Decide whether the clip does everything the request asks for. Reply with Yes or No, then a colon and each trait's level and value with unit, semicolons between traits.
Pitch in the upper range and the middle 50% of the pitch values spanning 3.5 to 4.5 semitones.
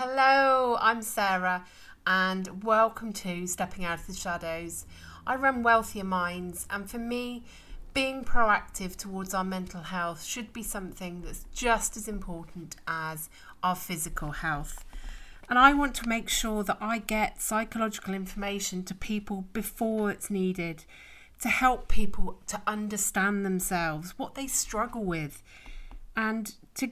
Yes: high, 200 Hz; average, 4.0 semitones